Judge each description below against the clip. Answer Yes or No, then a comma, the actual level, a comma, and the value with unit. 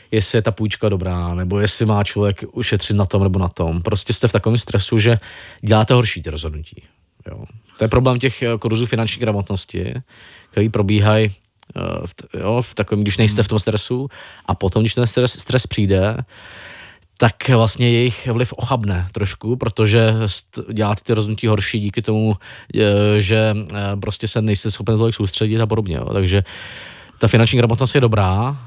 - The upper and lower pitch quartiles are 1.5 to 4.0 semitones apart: Yes, narrow, 2.4 semitones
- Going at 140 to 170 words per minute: Yes, average, 165 wpm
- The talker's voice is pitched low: Yes, low, 110 Hz